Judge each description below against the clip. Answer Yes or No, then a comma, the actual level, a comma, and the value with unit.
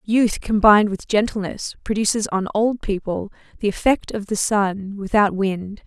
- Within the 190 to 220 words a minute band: No, average, 155 wpm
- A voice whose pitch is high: Yes, high, 205 Hz